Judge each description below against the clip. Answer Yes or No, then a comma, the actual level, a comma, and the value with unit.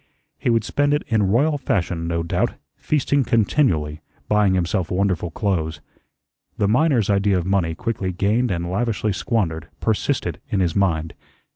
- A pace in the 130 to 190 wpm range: Yes, average, 150 wpm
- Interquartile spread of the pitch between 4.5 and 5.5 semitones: Yes, average, 5.1 semitones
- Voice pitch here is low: Yes, low, 100 Hz